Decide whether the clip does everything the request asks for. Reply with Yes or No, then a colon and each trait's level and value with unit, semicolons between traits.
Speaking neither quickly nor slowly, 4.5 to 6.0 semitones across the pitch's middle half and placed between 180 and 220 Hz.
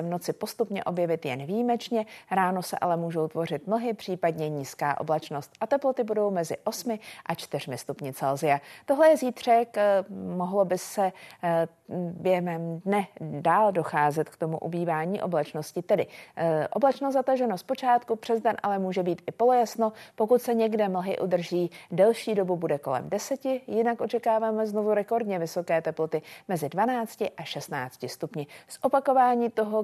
Yes: average, 150 wpm; wide, 5.4 semitones; high, 190 Hz